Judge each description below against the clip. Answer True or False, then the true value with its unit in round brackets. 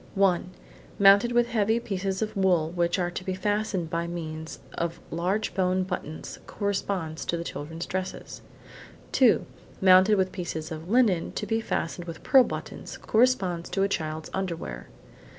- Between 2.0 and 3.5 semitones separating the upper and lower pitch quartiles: True (3.2 semitones)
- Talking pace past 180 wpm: False (145 wpm)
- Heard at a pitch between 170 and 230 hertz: True (185 Hz)